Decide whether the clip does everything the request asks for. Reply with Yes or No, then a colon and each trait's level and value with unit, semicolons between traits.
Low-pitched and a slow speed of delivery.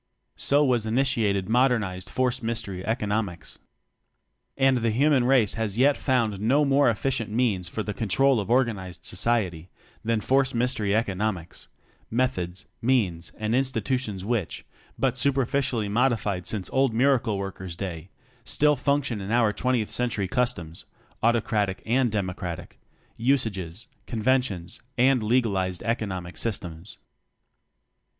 Yes: low, 115 Hz; slow, 130 wpm